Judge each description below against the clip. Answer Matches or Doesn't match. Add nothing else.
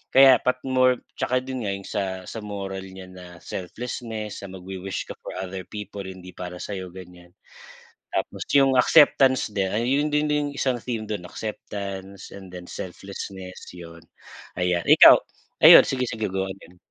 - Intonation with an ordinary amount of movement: Matches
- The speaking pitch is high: Doesn't match